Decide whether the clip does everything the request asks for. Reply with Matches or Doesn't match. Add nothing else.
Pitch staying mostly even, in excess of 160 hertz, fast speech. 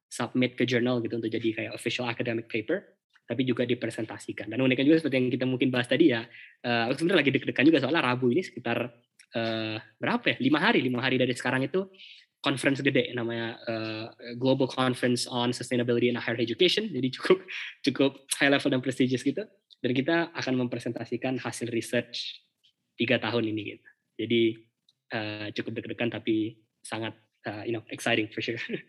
Doesn't match